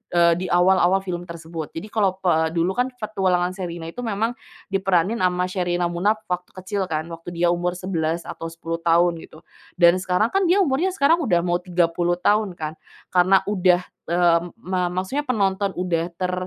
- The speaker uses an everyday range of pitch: No, narrow, 2.3 semitones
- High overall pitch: No, medium, 180 Hz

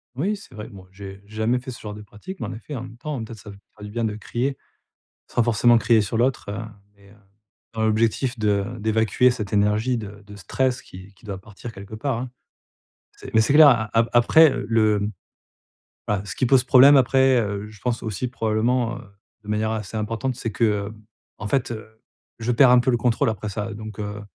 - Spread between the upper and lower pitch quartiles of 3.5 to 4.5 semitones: No, average, 2.8 semitones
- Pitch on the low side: Yes, low, 110 Hz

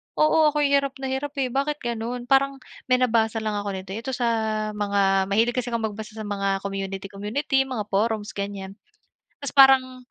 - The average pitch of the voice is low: No, high, 230 Hz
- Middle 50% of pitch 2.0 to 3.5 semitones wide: No, average, 4.8 semitones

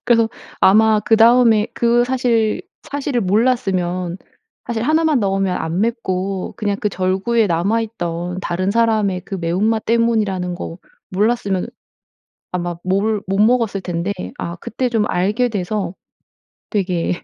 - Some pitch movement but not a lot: Yes, average, 3.9 semitones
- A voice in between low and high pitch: No, high, 205 Hz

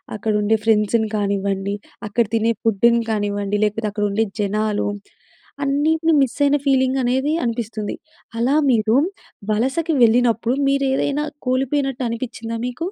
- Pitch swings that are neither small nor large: Yes, average, 3.9 semitones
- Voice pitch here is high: Yes, high, 230 Hz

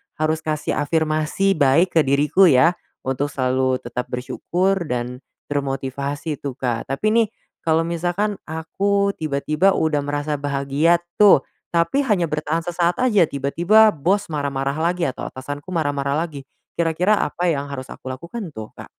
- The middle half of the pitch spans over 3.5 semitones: Yes, average, 3.9 semitones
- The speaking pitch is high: No, medium, 155 Hz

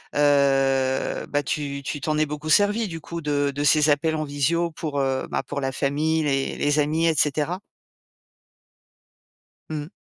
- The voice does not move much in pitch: Yes, narrow, 2.0 semitones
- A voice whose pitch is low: No, medium, 145 Hz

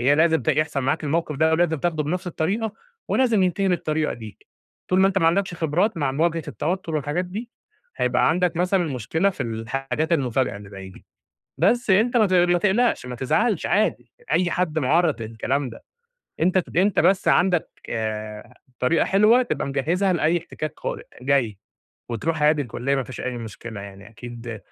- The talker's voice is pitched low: No, medium, 160 Hz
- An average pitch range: No, wide, 6.2 semitones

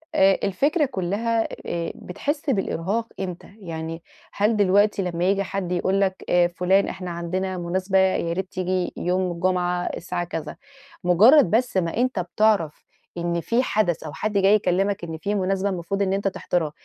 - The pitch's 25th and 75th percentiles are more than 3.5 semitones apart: No, narrow, 2.5 semitones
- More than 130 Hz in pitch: Yes, medium, 185 Hz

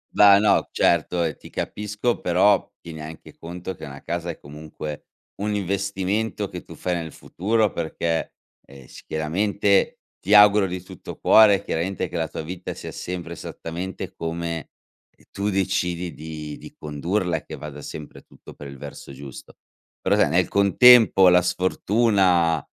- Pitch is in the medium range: No, very low, 90 Hz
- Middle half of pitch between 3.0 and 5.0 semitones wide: Yes, average, 3.8 semitones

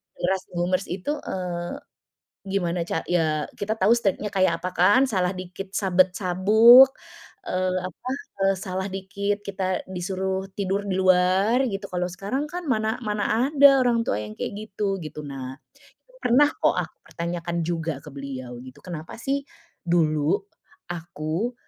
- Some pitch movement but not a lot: Yes, average, 3.2 semitones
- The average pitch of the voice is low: No, medium, 185 Hz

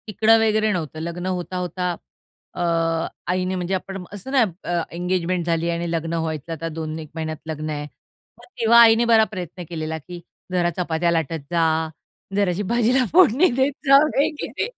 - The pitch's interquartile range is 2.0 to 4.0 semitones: No, average, 4.6 semitones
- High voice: No, medium, 180 Hz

